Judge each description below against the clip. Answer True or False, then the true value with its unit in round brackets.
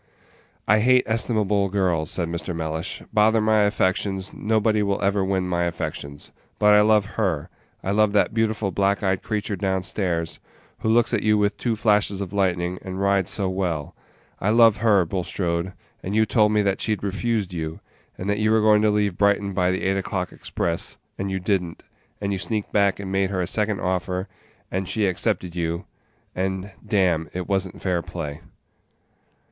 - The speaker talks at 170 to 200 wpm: True (185 wpm)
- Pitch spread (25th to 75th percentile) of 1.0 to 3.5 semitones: True (2.5 semitones)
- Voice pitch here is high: False (100 Hz)